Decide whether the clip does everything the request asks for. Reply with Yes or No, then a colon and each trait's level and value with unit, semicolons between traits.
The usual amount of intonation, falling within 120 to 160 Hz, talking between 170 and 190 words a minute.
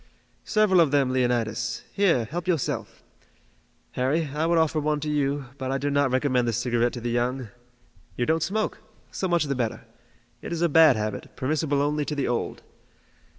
Yes: average, 4.5 semitones; medium, 140 Hz; average, 180 wpm